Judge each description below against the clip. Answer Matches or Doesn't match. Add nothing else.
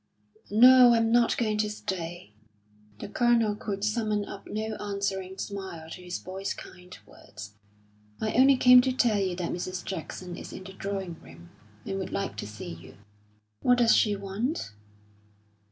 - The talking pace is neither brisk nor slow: Matches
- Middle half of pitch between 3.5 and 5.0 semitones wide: Matches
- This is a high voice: Matches